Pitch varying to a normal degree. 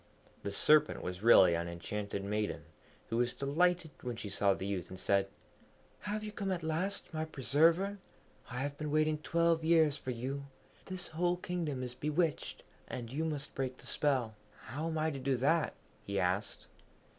No: wide, 6.3 semitones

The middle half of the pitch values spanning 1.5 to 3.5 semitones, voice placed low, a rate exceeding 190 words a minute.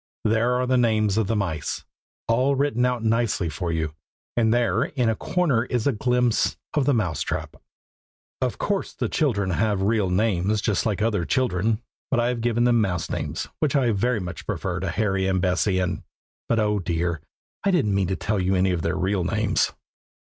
No: average, 4.4 semitones; low, 110 Hz; average, 200 wpm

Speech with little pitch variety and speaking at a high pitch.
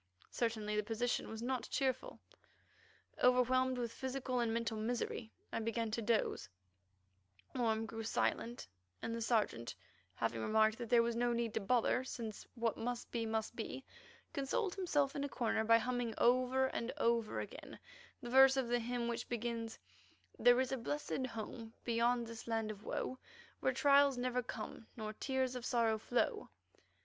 Yes: narrow, 2.1 semitones; high, 235 Hz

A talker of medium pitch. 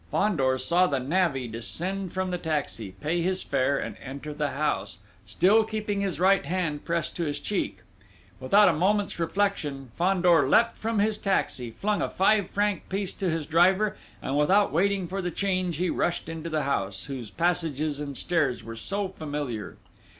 Yes: medium, 170 Hz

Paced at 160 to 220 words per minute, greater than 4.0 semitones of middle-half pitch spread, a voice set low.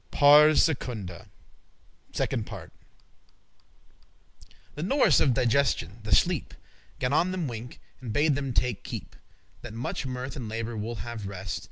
No: average, 150 wpm; average, 4.6 semitones; low, 125 Hz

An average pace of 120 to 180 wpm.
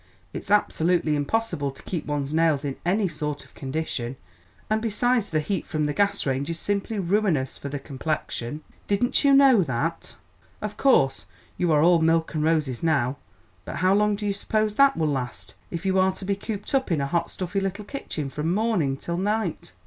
No: average, 195 wpm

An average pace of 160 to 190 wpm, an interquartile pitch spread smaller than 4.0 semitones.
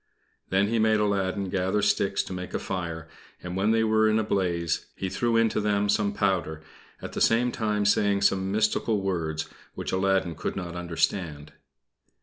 Yes: average, 175 wpm; average, 2.8 semitones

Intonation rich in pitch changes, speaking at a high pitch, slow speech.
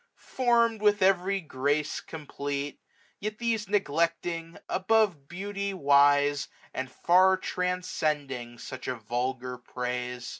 No: wide, 6.6 semitones; medium, 160 Hz; slow, 105 wpm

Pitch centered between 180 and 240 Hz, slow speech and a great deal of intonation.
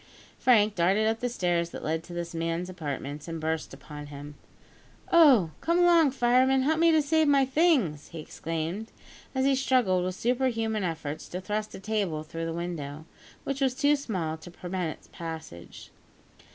No: medium, 185 Hz; average, 180 wpm; wide, 8.1 semitones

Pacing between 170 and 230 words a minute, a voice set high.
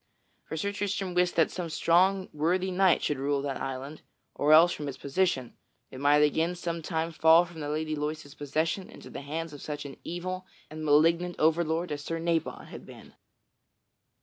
No: average, 185 wpm; medium, 160 Hz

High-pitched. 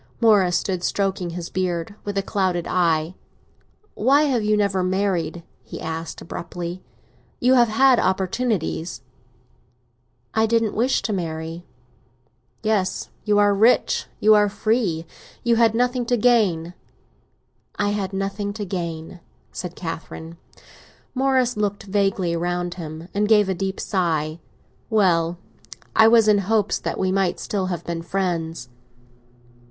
Yes: high, 195 Hz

